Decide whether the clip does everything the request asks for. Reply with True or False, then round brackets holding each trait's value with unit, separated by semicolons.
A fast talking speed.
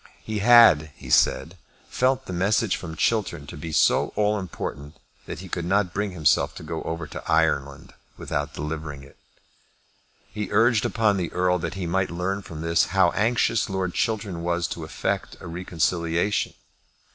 False (170 wpm)